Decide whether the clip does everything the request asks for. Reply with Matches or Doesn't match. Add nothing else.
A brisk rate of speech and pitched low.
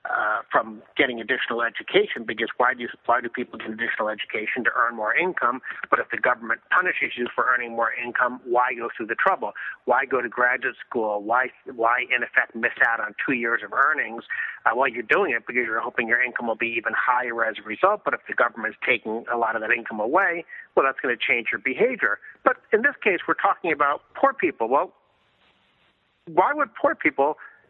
Matches